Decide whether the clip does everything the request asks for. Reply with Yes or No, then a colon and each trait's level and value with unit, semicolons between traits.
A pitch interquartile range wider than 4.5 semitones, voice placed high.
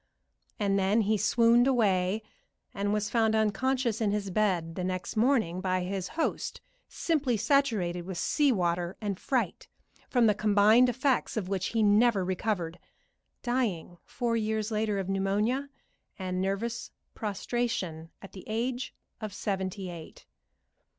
No: average, 3.8 semitones; high, 210 Hz